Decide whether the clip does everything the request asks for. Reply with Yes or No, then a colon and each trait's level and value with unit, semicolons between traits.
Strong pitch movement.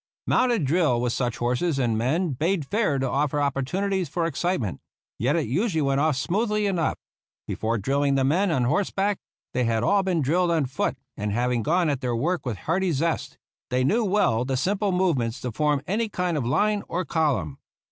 Yes: wide, 6.4 semitones